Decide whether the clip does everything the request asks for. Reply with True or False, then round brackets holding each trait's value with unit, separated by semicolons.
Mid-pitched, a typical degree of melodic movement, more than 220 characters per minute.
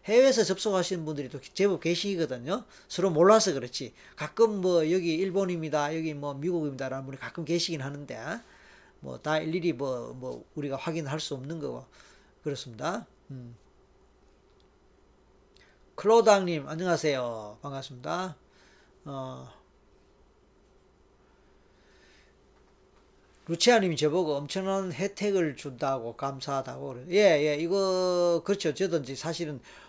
True (160 Hz; 5.0 semitones; 265 characters per minute)